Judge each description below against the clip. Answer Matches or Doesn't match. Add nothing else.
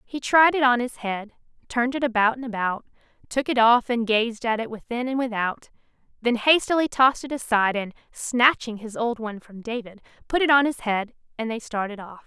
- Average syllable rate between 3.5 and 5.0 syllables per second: Doesn't match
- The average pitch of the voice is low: Doesn't match